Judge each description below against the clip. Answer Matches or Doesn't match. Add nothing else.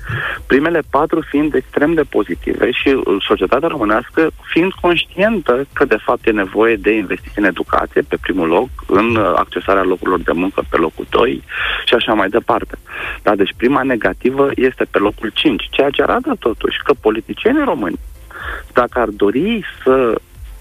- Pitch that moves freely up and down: Matches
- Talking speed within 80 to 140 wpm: Doesn't match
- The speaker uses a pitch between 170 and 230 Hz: Doesn't match